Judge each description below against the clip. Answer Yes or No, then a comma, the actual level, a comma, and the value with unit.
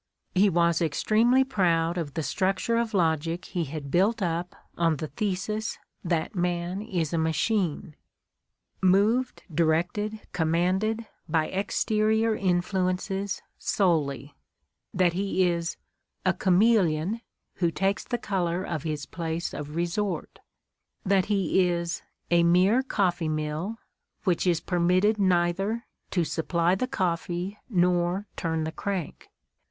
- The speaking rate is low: Yes, slow, 125 wpm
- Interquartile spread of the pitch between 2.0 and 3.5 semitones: Yes, average, 3.2 semitones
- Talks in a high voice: No, medium, 180 Hz